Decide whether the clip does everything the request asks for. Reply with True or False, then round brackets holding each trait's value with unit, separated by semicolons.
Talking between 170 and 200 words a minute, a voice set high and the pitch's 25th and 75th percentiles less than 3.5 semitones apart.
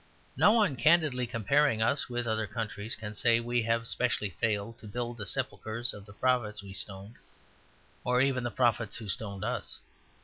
False (175 wpm; 115 Hz; 2.9 semitones)